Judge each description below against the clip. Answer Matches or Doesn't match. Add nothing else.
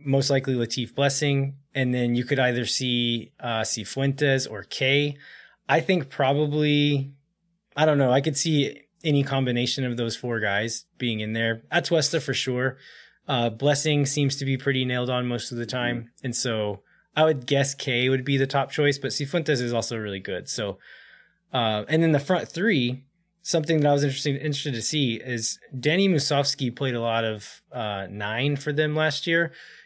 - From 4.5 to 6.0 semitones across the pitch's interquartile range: Doesn't match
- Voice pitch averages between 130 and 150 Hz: Matches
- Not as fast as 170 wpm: Doesn't match